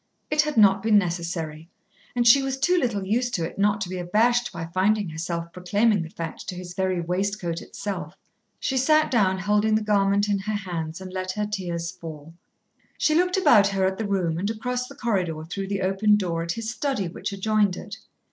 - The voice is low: No, high, 195 Hz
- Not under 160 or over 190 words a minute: No, fast, 205 wpm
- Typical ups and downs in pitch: Yes, average, 3.6 semitones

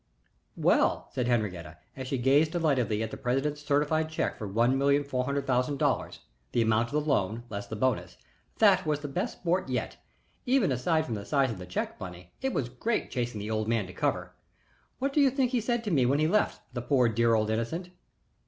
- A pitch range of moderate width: No, wide, 5.7 semitones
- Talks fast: Yes, fast, 220 wpm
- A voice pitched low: Yes, low, 130 Hz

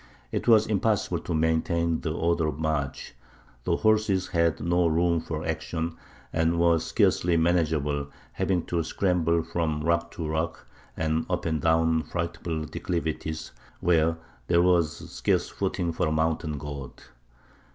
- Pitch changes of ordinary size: No, narrow, 1.4 semitones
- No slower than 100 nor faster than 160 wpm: Yes, average, 140 wpm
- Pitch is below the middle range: Yes, very low, 80 Hz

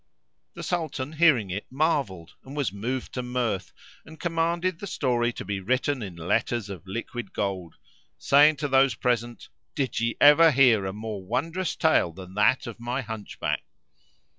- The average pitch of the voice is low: Yes, low, 125 Hz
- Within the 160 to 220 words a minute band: Yes, average, 165 wpm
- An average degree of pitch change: No, wide, 6.0 semitones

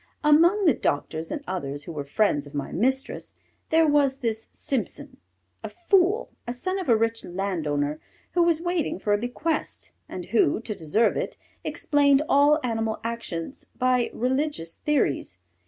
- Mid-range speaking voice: No, high, 240 Hz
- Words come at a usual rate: Yes, average, 155 wpm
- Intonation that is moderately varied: No, wide, 8.9 semitones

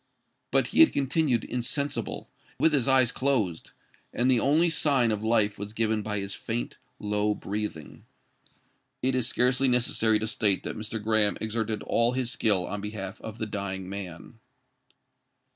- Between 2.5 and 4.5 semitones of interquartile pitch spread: Yes, average, 3.4 semitones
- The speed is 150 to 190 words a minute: Yes, average, 155 wpm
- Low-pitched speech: Yes, low, 110 Hz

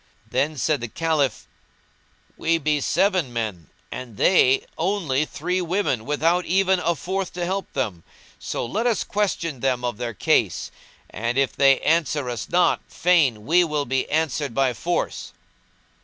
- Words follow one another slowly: No, average, 155 wpm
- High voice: No, medium, 150 Hz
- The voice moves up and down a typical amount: No, wide, 5.8 semitones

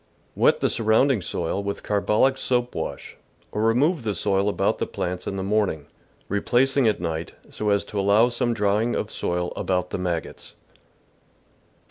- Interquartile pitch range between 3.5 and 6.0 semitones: Yes, average, 4.1 semitones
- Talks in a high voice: No, low, 105 Hz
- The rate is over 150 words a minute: Yes, average, 170 wpm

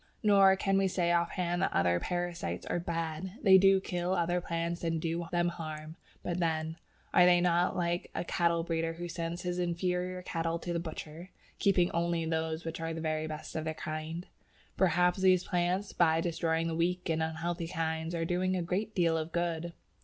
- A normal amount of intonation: No, narrow, 1.6 semitones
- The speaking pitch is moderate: Yes, medium, 170 Hz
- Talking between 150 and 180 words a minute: No, average, 195 wpm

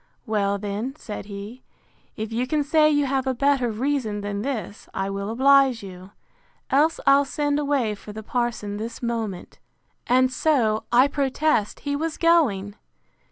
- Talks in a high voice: Yes, high, 240 Hz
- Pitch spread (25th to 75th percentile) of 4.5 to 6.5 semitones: Yes, average, 5.1 semitones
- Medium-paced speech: Yes, average, 160 wpm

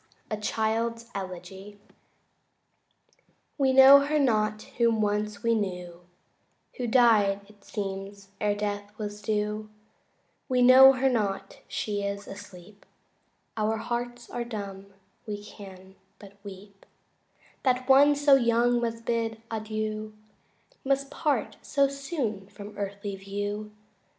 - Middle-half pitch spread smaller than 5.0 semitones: Yes, average, 3.0 semitones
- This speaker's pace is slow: Yes, slow, 120 wpm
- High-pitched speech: Yes, high, 215 Hz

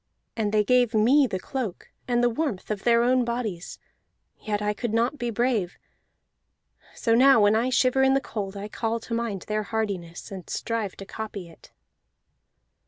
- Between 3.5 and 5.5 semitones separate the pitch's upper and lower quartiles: No, average, 2.9 semitones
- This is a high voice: Yes, high, 225 Hz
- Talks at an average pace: Yes, average, 175 wpm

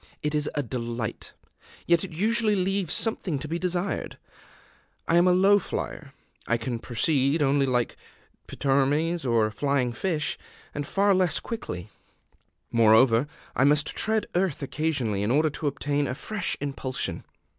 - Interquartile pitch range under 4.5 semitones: No, wide, 5.4 semitones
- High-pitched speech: No, medium, 145 Hz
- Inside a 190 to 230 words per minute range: No, average, 155 wpm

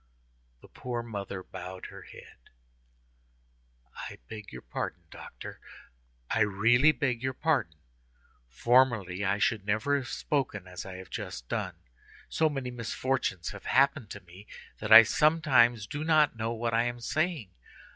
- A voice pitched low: Yes, low, 115 Hz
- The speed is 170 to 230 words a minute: No, average, 145 wpm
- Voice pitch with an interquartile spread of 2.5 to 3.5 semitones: No, average, 5.0 semitones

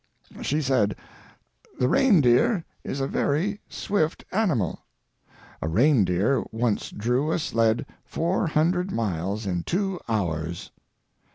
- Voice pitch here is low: Yes, low, 130 Hz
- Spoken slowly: Yes, slow, 110 wpm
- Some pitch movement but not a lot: No, wide, 8.0 semitones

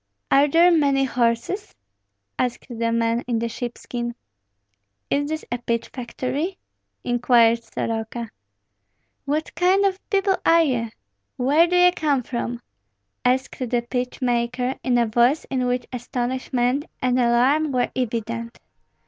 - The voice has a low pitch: No, very high, 250 Hz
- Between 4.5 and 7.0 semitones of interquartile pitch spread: No, average, 3.3 semitones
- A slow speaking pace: Yes, slow, 130 wpm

